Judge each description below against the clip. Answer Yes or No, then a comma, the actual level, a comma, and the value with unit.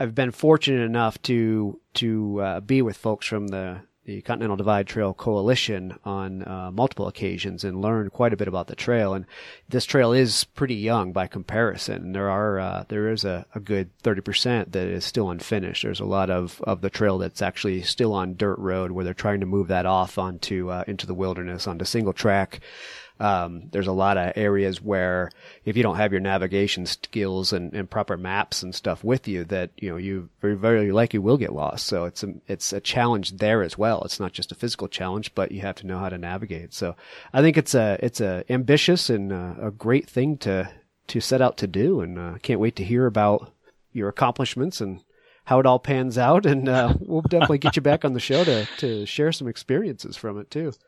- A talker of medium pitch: No, low, 105 Hz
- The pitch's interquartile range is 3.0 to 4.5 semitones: Yes, average, 4.1 semitones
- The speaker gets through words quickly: Yes, fast, 220 wpm